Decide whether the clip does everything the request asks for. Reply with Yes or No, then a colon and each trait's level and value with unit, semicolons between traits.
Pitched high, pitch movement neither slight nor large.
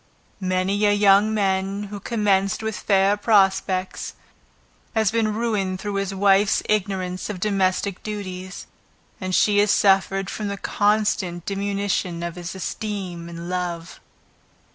No: high, 195 Hz; narrow, 1.8 semitones